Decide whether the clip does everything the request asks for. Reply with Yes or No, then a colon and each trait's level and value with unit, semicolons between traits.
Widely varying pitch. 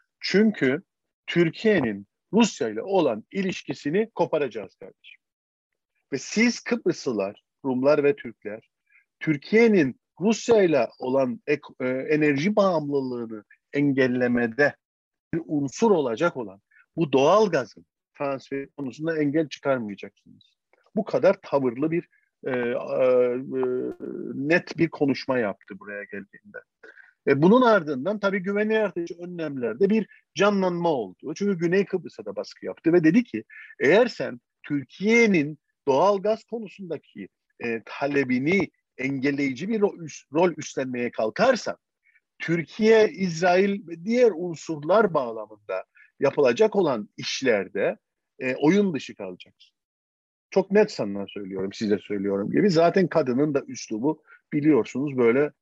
Yes: wide, 7.7 semitones